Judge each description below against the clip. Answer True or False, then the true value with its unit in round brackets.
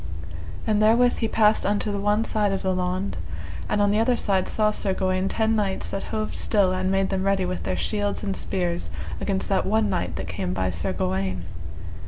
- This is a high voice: True (195 Hz)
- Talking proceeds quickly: True (210 wpm)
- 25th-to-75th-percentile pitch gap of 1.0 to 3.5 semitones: True (2.5 semitones)